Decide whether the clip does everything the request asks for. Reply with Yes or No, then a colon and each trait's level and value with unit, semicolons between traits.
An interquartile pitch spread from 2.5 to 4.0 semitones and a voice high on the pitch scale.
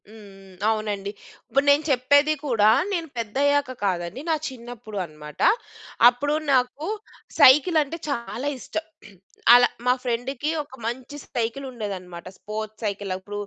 No: average, 5.2 semitones; high, 240 Hz